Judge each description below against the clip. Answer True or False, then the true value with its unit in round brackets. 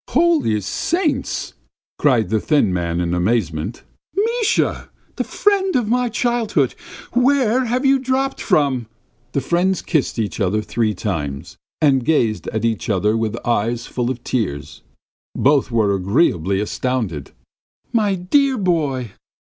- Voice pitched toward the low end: True (130 Hz)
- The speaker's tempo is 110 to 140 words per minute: True (135 wpm)